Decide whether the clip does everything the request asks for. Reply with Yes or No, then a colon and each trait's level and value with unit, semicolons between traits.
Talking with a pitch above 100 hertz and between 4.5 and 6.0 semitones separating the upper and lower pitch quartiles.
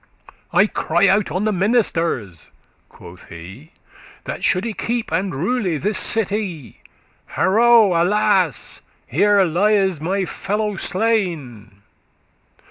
Yes: high, 190 Hz; average, 5.0 semitones